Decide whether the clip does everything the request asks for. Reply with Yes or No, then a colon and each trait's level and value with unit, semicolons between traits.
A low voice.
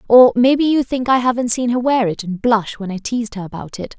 No: high, 235 Hz